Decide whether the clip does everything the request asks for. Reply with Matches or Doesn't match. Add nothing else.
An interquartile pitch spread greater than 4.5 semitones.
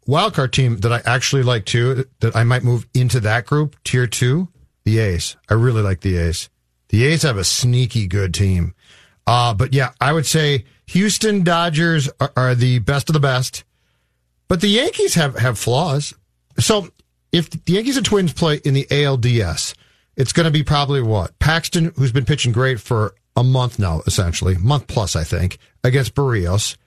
Matches